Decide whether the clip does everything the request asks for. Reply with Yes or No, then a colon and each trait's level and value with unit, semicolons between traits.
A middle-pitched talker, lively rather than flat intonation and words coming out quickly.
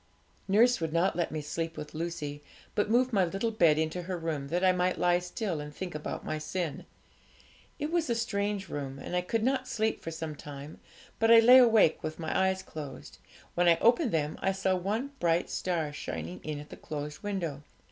No: medium, 175 Hz; average, 5.0 semitones; fast, 210 wpm